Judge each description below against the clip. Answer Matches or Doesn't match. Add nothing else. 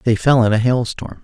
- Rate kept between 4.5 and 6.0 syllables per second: Matches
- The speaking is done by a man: Matches